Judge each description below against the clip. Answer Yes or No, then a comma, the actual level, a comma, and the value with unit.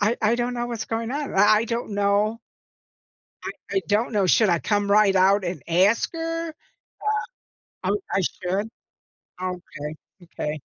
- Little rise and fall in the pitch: No, average, 3.6 semitones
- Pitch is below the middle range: No, high, 205 Hz